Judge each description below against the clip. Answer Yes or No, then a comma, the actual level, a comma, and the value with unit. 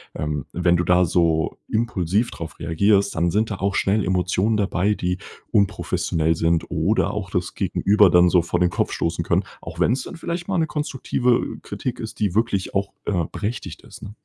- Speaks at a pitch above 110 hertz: No, very low, 95 Hz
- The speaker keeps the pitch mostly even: No, average, 3.7 semitones